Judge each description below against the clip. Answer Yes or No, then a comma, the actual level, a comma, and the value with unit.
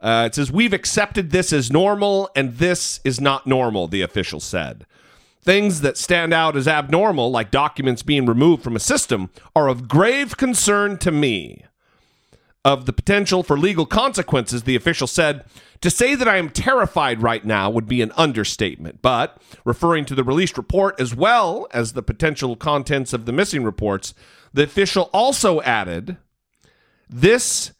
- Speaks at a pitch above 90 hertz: Yes, medium, 140 Hz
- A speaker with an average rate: Yes, average, 165 wpm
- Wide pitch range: Yes, wide, 6.8 semitones